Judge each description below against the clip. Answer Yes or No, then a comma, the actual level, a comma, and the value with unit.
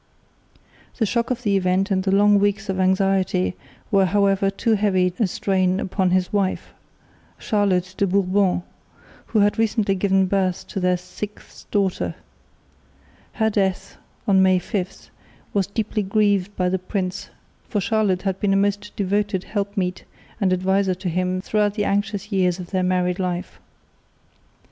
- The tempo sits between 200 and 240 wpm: No, average, 155 wpm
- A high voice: Yes, high, 195 Hz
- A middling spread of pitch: No, narrow, 1.8 semitones